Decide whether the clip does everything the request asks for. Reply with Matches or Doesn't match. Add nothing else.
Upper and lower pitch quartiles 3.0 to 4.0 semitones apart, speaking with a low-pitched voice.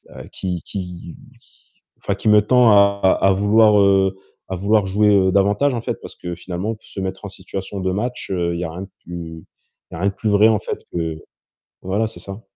Doesn't match